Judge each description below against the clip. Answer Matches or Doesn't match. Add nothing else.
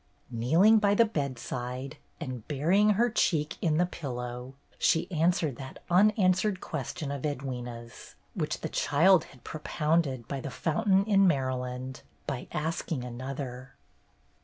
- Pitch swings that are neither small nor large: Doesn't match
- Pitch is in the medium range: Matches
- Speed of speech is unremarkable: Doesn't match